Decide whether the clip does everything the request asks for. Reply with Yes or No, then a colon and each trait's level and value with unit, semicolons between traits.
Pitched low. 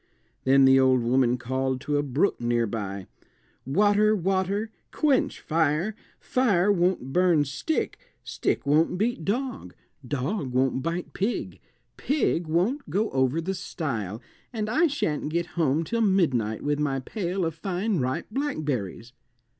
No: medium, 160 Hz